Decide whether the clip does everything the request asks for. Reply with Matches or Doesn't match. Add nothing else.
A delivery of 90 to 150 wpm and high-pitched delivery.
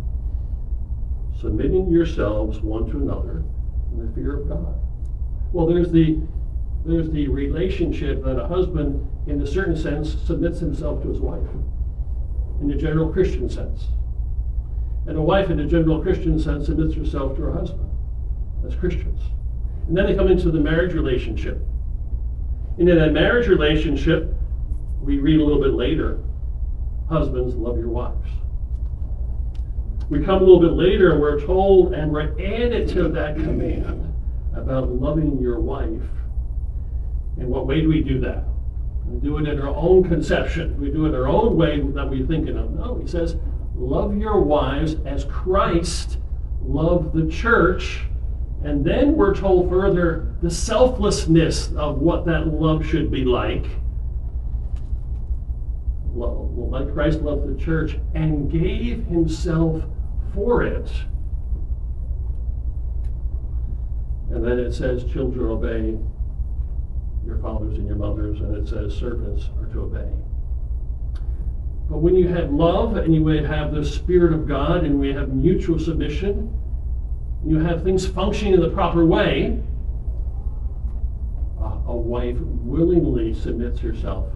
Doesn't match